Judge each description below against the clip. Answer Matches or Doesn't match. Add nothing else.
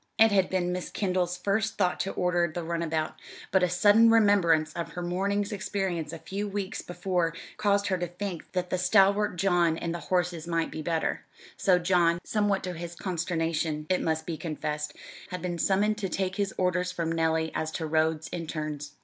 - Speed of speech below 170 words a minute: Doesn't match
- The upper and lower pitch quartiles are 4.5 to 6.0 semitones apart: Doesn't match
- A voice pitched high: Doesn't match